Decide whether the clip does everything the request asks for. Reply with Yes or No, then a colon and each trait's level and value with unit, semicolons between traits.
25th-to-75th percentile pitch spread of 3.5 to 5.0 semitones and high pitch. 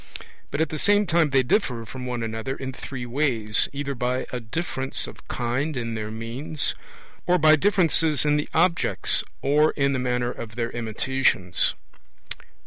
No: average, 4.3 semitones; low, 130 Hz